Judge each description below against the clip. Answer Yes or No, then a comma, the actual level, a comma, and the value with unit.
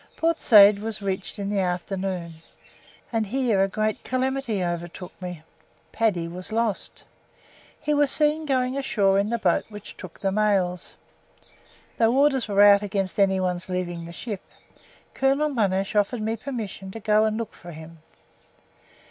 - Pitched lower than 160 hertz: No, high, 205 Hz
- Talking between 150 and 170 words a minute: Yes, average, 155 wpm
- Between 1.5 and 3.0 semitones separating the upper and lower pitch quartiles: No, average, 3.9 semitones